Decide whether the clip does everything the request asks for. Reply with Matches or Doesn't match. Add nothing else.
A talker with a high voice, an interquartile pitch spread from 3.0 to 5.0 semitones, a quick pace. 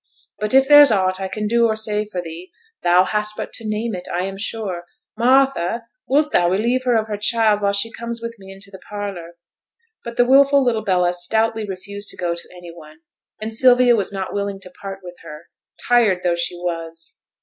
Matches